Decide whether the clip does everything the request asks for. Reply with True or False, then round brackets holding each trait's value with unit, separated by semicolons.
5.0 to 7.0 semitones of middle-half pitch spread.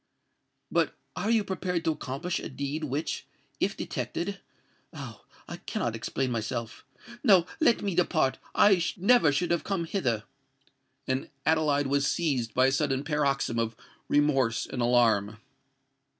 True (5.4 semitones)